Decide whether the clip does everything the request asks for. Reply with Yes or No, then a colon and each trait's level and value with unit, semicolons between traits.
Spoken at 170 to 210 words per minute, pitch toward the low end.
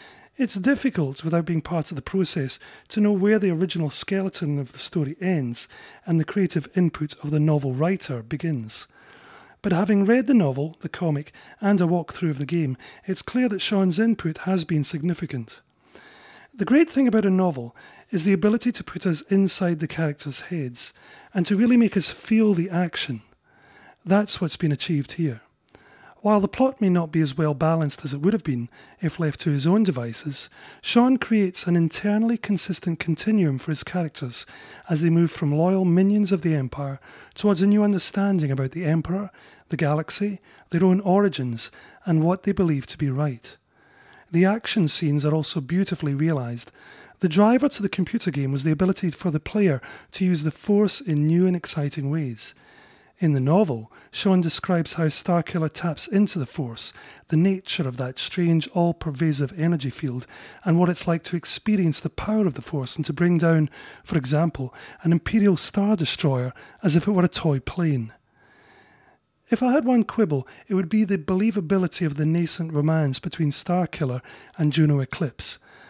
No: average, 180 wpm; medium, 170 Hz